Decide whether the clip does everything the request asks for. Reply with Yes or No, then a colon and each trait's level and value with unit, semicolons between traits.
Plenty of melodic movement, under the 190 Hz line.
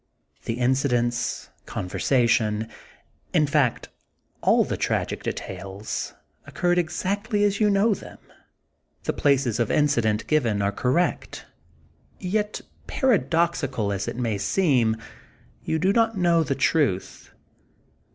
Yes: wide, 7.5 semitones; medium, 140 Hz